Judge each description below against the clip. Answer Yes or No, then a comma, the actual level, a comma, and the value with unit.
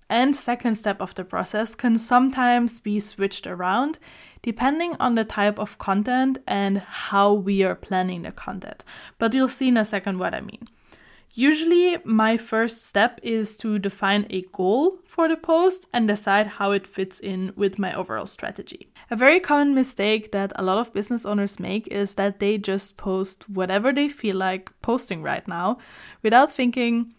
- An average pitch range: Yes, average, 3.8 semitones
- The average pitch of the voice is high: Yes, high, 215 Hz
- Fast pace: No, average, 175 wpm